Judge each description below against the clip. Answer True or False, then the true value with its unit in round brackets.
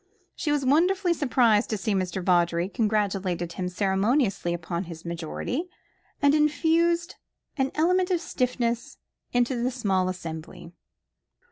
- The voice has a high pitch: True (225 Hz)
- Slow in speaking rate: True (125 wpm)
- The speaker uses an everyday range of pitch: False (8.3 semitones)